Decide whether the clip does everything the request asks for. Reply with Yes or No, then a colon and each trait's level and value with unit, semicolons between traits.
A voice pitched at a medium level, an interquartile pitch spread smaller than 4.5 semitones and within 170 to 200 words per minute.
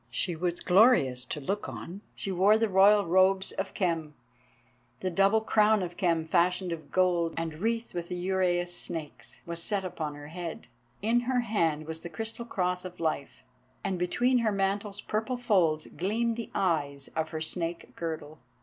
Yes: medium, 180 Hz; average, 3.8 semitones; average, 175 wpm